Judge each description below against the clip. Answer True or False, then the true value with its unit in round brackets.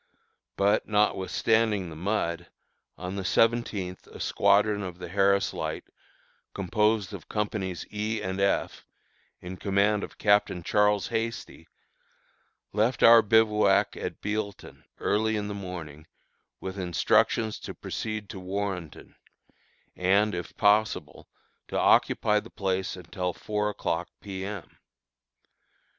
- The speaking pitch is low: True (100 Hz)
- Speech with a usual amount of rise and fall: False (2.3 semitones)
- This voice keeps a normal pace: False (120 wpm)